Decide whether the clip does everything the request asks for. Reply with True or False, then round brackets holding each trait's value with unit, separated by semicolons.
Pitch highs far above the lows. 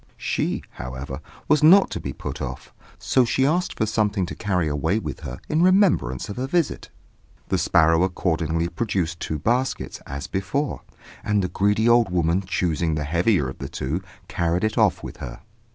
True (6.3 semitones)